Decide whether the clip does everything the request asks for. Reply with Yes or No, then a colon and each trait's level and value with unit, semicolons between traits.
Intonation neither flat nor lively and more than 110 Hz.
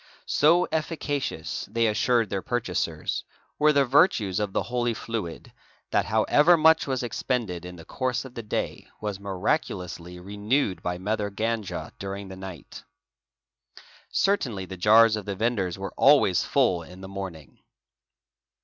No: average, 4.8 semitones; low, 105 Hz